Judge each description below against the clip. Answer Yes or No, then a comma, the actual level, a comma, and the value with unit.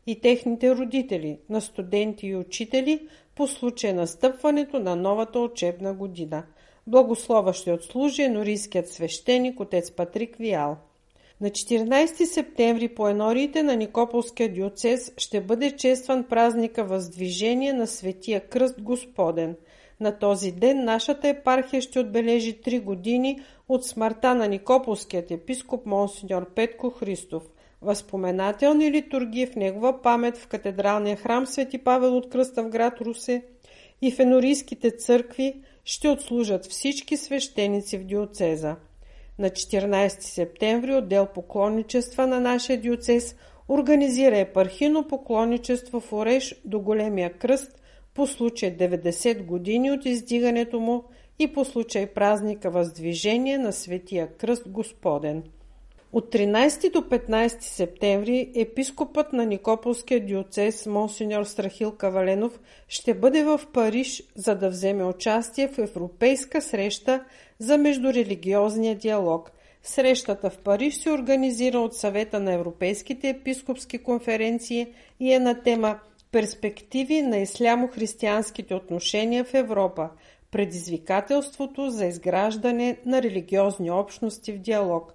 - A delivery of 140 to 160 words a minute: No, average, 120 wpm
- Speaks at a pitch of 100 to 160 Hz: No, high, 230 Hz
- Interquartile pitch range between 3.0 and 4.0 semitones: No, average, 4.4 semitones